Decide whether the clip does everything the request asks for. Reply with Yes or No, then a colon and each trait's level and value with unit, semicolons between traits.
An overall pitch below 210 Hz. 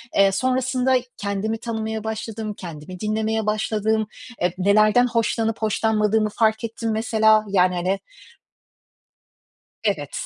No: high, 220 Hz